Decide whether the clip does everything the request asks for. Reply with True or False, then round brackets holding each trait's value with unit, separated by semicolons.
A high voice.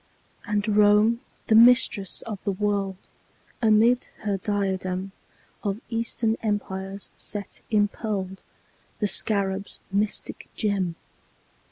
True (205 Hz)